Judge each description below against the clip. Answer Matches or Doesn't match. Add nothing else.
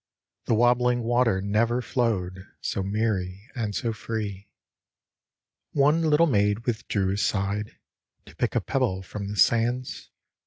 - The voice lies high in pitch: Doesn't match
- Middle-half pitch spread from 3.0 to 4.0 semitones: Matches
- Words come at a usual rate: Doesn't match